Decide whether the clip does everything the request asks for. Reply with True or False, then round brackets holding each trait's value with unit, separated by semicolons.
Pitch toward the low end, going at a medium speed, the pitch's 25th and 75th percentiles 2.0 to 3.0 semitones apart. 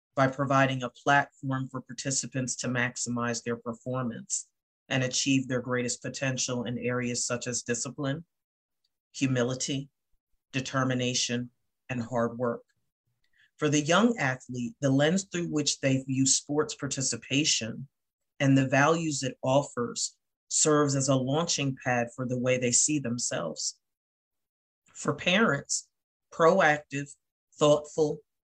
False (130 Hz; 120 wpm; 2.6 semitones)